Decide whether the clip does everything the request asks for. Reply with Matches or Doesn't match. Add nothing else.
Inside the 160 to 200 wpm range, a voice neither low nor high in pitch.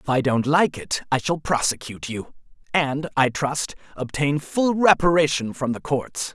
Matches